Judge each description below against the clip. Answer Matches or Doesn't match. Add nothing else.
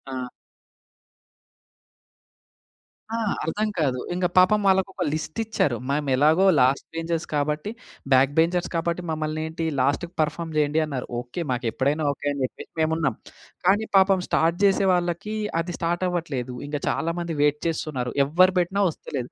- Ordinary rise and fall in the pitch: Matches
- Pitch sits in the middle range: Matches